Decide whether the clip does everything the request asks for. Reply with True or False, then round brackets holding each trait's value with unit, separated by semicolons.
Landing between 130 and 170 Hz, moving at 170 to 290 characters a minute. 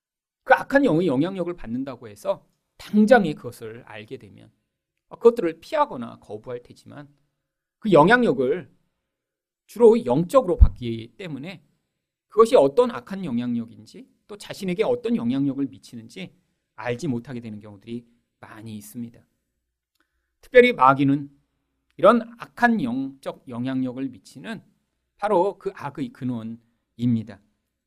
True (135 Hz; 275 characters per minute)